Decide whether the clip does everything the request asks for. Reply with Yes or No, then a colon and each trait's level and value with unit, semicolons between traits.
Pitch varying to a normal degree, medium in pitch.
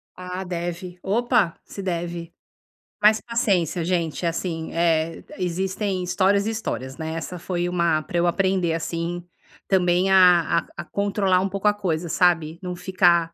No: narrow, 2.3 semitones; medium, 180 Hz